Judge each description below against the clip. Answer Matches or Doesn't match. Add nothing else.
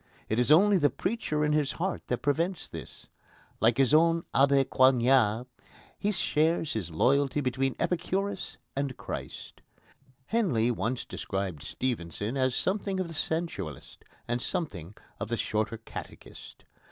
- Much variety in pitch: Matches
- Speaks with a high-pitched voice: Doesn't match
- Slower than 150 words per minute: Matches